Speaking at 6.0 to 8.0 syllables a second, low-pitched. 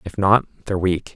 Yes: 6.1 syllables/s; very low, 95 Hz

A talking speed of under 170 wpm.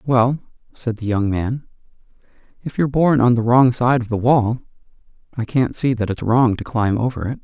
No: average, 200 wpm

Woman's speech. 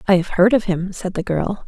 Yes: female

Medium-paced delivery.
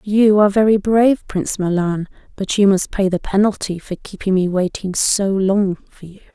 Yes: average, 190 wpm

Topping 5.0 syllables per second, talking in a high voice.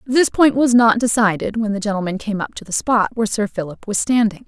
Yes: 5.8 syllables/s; high, 215 Hz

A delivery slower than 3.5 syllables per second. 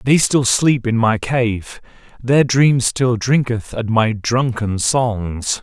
Yes: 3.1 syllables/s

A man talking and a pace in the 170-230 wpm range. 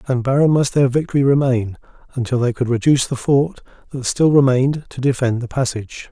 Yes: male; average, 185 wpm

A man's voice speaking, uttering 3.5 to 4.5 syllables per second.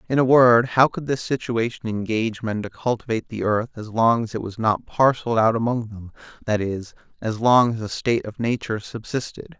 No: male; 5.5 syllables/s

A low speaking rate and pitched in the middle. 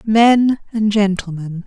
No: slow, 110 wpm; high, 210 Hz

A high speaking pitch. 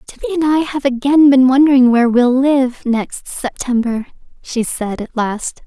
Yes: very high, 260 Hz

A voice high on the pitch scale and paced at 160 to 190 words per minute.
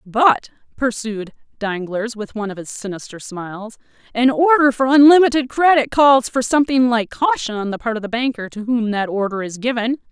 Yes: high, 235 Hz; average, 185 wpm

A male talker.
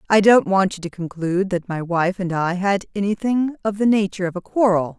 No: female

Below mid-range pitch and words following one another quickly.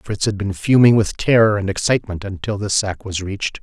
Yes: low, 100 Hz; fast, 215 wpm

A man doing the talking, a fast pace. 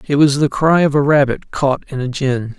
Yes: male; fast, 255 wpm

